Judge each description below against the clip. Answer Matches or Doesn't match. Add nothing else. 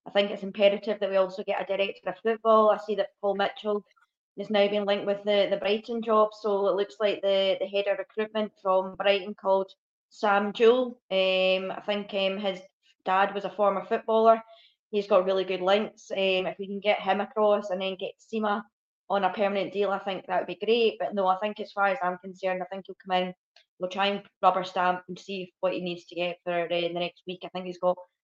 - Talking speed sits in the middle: Doesn't match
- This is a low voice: Doesn't match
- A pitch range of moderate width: Doesn't match